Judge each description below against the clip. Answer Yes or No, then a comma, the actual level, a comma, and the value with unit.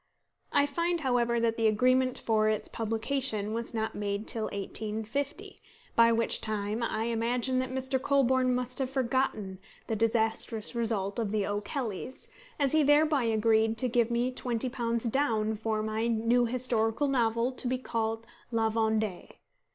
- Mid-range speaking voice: No, high, 230 Hz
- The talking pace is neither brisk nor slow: Yes, average, 150 wpm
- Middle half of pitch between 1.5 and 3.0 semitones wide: Yes, narrow, 2.6 semitones